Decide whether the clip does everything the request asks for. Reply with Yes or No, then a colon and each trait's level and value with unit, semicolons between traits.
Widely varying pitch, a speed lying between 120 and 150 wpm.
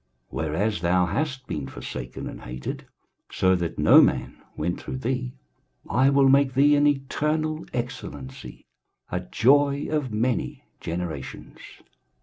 Yes: wide, 7.9 semitones; slow, 135 wpm